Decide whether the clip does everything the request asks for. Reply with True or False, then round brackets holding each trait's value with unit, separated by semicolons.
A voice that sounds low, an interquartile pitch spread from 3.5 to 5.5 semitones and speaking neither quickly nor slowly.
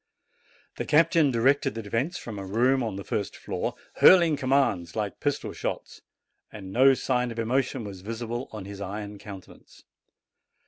True (115 Hz; 4.7 semitones; 155 wpm)